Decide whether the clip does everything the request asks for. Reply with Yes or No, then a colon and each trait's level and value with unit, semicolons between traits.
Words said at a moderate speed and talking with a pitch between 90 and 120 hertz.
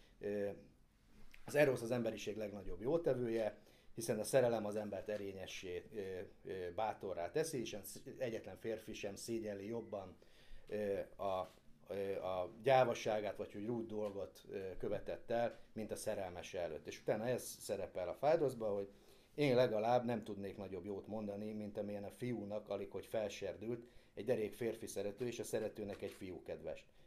Yes: average, 145 wpm; low, 105 Hz